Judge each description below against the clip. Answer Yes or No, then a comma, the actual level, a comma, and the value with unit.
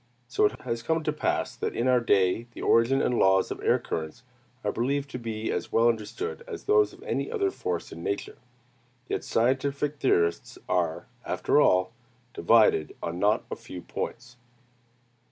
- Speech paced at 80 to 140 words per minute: No, average, 170 wpm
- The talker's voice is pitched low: Yes, low, 120 Hz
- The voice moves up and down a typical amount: No, wide, 6.4 semitones